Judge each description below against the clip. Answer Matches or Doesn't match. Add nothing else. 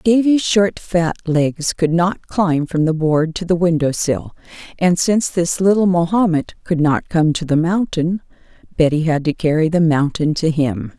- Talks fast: Doesn't match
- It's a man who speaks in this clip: Doesn't match